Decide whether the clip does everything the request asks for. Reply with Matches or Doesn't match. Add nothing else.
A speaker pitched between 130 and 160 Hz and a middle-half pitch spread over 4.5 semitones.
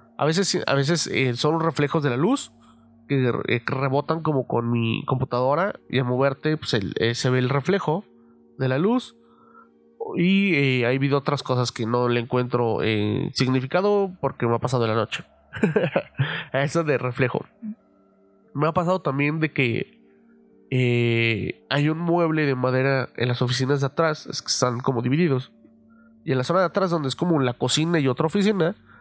Matches